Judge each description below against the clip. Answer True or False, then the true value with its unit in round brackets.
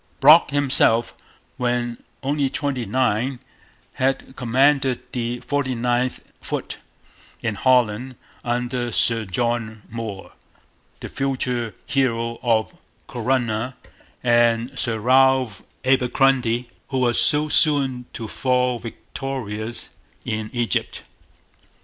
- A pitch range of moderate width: False (2.3 semitones)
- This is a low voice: True (125 Hz)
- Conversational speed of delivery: False (95 wpm)